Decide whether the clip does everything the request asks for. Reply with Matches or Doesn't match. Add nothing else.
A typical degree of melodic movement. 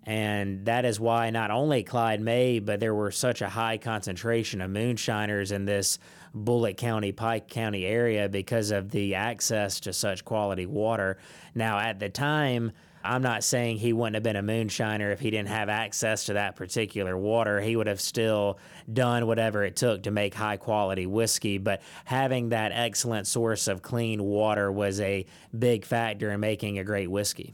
Doesn't match